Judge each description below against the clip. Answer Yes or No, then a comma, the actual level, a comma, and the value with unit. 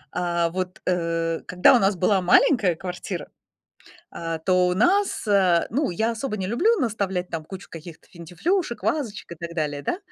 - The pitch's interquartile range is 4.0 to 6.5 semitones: Yes, average, 4.4 semitones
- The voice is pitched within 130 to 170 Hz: No, medium, 185 Hz